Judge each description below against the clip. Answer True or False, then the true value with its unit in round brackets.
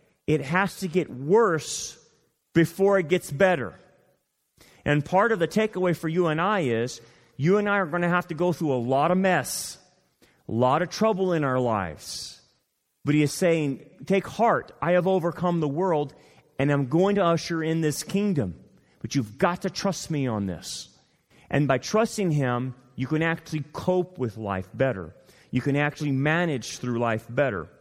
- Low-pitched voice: False (155 Hz)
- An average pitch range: False (5.7 semitones)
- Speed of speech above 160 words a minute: True (185 wpm)